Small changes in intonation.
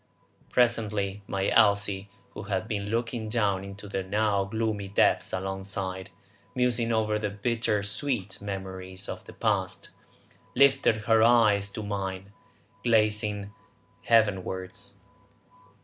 Yes: narrow, 2.3 semitones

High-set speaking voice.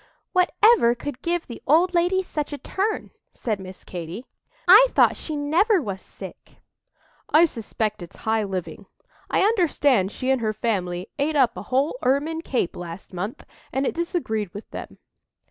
Yes: very high, 265 Hz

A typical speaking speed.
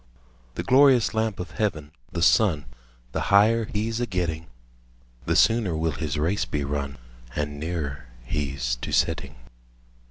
Yes: average, 160 wpm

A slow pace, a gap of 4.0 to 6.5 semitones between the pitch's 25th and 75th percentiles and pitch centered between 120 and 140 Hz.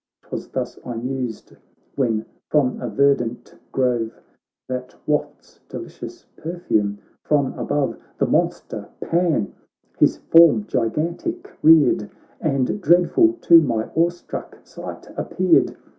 Yes: slow, 115 wpm; wide, 5.6 semitones; low, 135 Hz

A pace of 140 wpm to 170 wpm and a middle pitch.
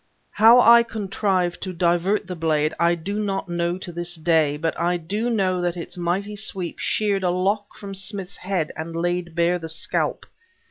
No: average, 185 wpm; medium, 180 Hz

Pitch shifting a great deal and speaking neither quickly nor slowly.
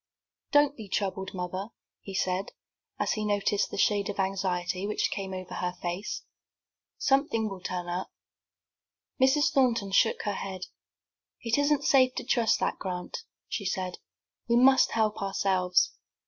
No: average, 3.9 semitones; average, 150 wpm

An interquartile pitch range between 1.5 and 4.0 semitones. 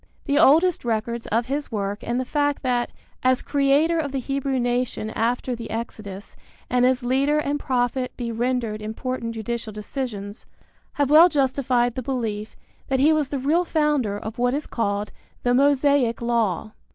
Yes: average, 3.4 semitones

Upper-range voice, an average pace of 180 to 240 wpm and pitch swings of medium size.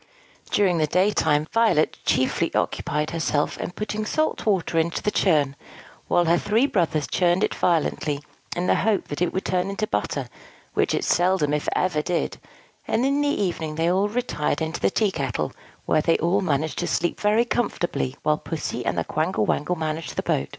No: medium, 175 Hz; average, 185 wpm; average, 4.7 semitones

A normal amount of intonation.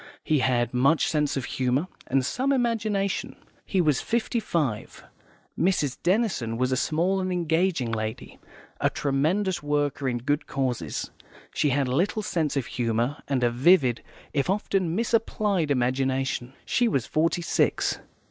No: wide, 6.5 semitones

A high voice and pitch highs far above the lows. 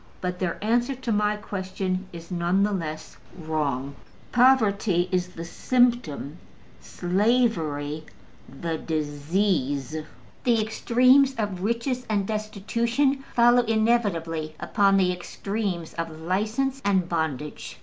Yes: high, 195 Hz; wide, 5.9 semitones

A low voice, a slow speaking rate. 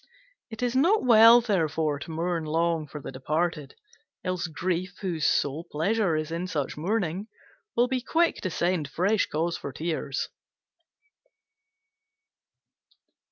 No: medium, 170 Hz; slow, 130 wpm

